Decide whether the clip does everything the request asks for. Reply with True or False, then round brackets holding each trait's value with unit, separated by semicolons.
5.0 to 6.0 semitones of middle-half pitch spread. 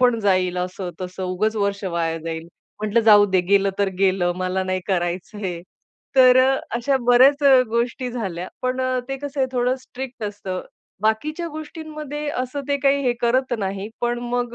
True (5.5 semitones)